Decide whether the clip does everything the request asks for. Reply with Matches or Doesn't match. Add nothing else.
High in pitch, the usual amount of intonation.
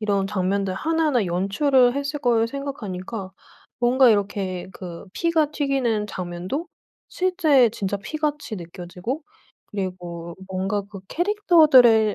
Doesn't match